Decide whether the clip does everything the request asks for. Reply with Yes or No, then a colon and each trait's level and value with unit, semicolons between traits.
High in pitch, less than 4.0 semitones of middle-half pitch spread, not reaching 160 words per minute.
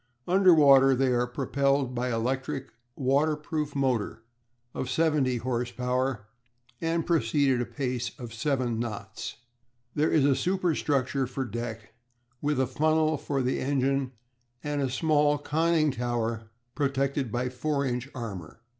No: low, 135 Hz; average, 3.1 semitones; average, 145 wpm